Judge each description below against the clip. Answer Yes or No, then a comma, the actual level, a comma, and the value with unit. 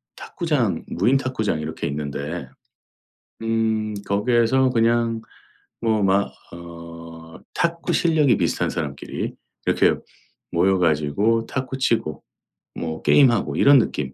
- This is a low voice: Yes, low, 105 Hz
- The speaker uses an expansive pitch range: Yes, wide, 6.2 semitones